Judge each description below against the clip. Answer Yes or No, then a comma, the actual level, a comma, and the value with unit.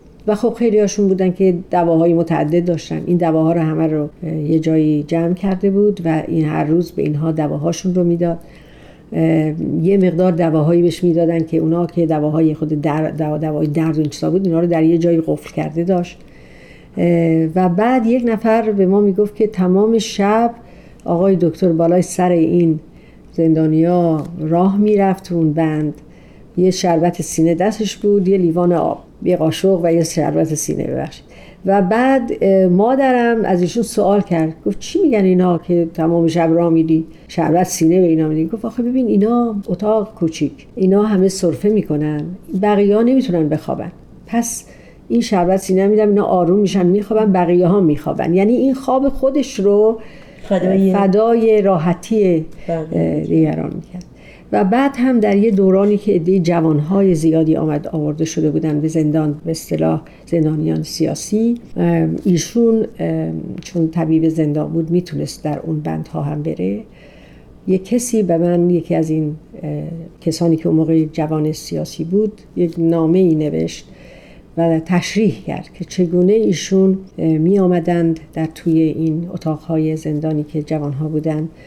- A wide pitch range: No, average, 3.7 semitones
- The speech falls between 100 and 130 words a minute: No, average, 150 wpm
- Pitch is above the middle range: No, medium, 170 Hz